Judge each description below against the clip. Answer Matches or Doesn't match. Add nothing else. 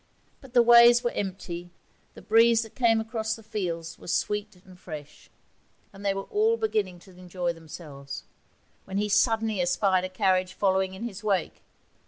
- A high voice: Matches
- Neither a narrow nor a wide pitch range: Matches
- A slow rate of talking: Doesn't match